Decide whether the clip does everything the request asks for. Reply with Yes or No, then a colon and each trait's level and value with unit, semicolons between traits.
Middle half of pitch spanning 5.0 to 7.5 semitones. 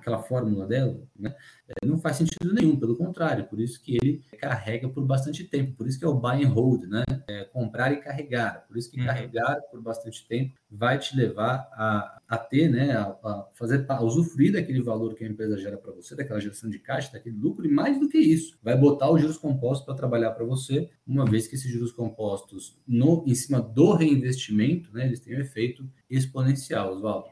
No: average, 3.6 semitones